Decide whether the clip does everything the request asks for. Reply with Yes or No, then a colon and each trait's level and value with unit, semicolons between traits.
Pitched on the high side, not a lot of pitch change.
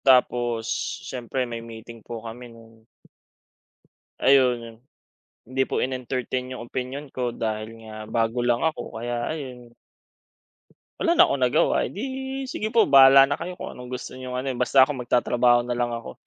No: low, 125 Hz; narrow, 2.2 semitones